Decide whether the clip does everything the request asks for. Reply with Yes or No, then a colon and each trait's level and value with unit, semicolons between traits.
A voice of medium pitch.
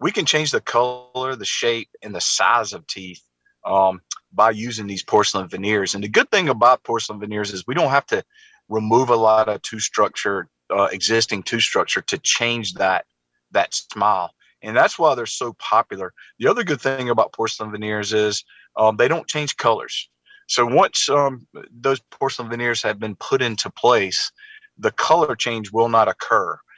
No: low, 115 Hz